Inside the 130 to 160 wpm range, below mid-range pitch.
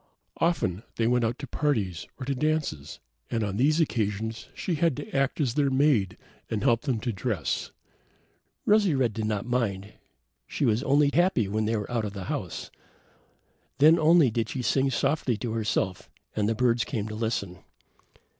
No: average, 180 wpm; low, 120 Hz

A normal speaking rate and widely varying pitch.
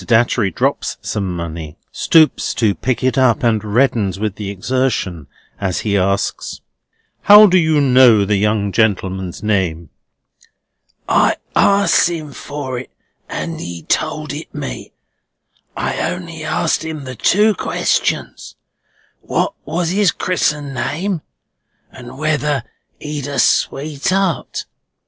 No: slow, 125 wpm; wide, 7.3 semitones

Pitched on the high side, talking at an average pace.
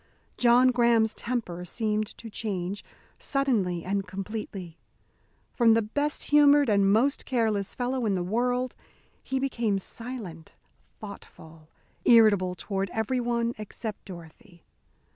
No: high, 220 Hz; slow, 115 wpm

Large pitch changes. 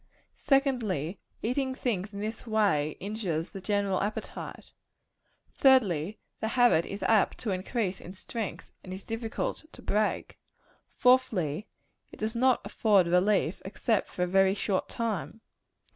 No: average, 3.5 semitones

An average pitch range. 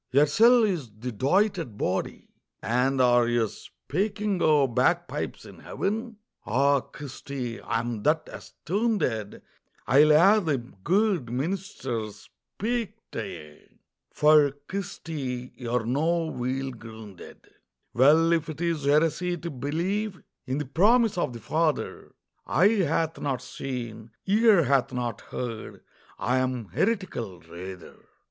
No: wide, 6.7 semitones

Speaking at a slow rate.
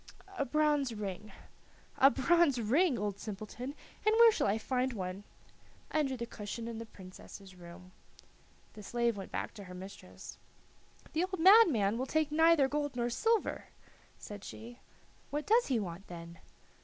No: average, 155 wpm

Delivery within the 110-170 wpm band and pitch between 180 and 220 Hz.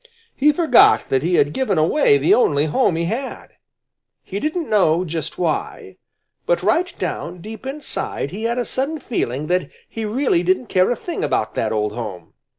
No: average, 180 wpm; high, 190 Hz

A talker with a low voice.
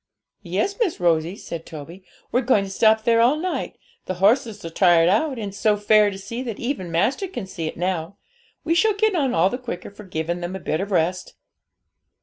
No: high, 200 Hz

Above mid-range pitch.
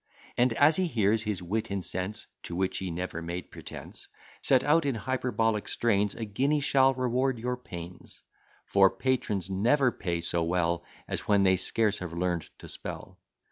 No: low, 105 Hz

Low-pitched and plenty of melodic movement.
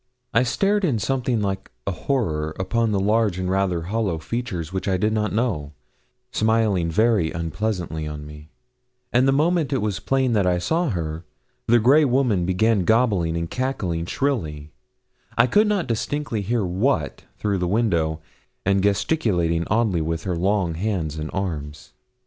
Yes: low, 100 Hz; wide, 5.9 semitones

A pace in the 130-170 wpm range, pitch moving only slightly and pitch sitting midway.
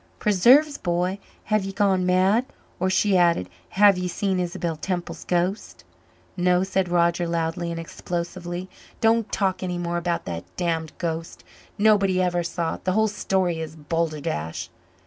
Yes: average, 150 wpm; narrow, 2.2 semitones; medium, 180 Hz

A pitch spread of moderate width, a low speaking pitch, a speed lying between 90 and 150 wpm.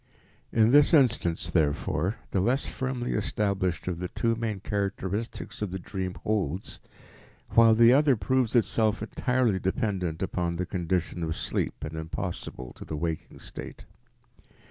Yes: average, 4.7 semitones; low, 100 Hz; average, 145 wpm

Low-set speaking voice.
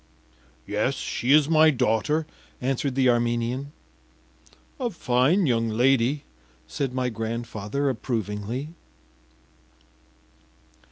Yes: low, 125 Hz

